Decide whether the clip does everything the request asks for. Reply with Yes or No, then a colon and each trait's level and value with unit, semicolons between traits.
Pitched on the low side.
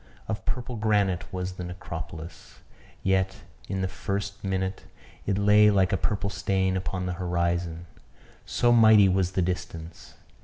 Yes: very low, 95 Hz